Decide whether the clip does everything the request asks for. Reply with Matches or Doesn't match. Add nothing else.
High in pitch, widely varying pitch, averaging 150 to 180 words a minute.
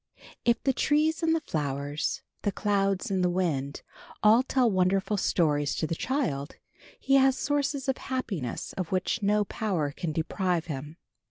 Matches